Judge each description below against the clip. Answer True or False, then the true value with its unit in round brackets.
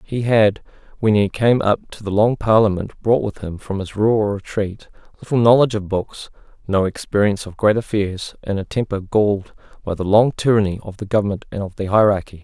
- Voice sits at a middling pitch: False (105 Hz)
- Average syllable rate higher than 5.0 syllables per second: True (5.5 syllables/s)